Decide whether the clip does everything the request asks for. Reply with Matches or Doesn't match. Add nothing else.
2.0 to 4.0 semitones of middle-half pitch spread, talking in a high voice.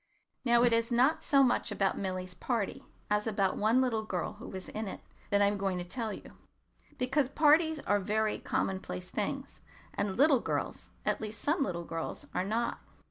Doesn't match